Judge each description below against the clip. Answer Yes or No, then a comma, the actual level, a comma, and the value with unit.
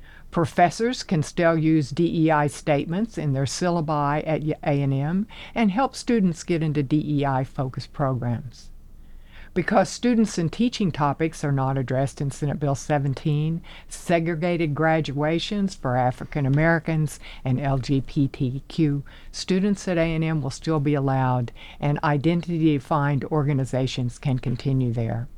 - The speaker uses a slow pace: Yes, slow, 120 wpm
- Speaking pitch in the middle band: Yes, medium, 150 Hz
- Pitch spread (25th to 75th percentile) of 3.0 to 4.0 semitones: Yes, average, 3.7 semitones